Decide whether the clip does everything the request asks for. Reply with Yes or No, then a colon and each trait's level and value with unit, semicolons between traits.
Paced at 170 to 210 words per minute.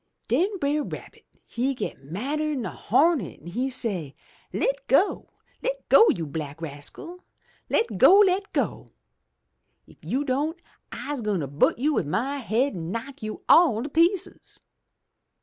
No: average, 150 wpm